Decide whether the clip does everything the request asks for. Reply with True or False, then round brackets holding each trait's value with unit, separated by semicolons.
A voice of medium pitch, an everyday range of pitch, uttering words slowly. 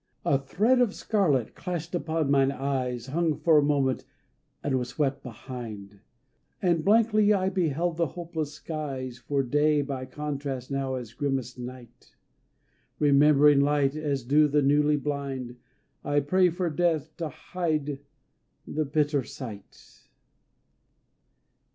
True (145 Hz; 3.2 semitones; 130 wpm)